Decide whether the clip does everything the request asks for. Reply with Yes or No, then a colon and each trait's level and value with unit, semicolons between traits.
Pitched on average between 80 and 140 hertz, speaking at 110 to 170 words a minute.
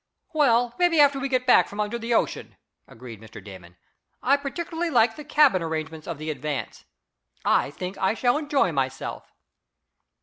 No: high, 225 Hz; average, 165 wpm